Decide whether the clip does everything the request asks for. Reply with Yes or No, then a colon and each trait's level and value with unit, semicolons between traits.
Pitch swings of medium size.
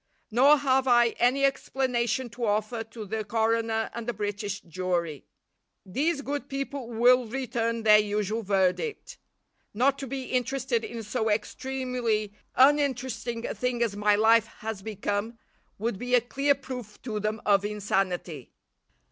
Yes: average, 3.5 semitones